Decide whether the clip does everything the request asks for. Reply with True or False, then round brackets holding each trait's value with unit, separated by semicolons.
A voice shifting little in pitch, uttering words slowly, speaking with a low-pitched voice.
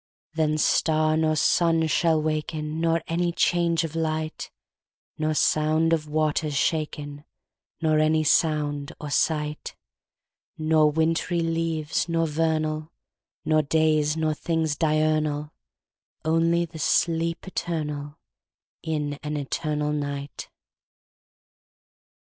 False (1.3 semitones; 85 wpm; 155 Hz)